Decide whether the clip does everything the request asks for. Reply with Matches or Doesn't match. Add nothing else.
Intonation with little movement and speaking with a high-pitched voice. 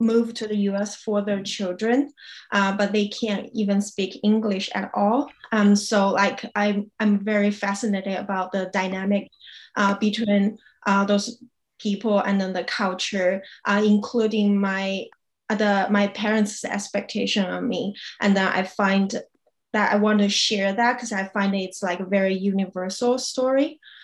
Matches